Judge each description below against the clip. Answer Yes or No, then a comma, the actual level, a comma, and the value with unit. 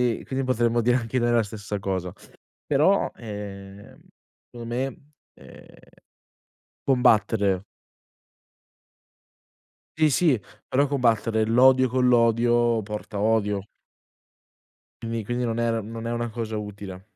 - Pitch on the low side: Yes, low, 115 Hz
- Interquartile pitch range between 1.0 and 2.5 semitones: No, average, 2.9 semitones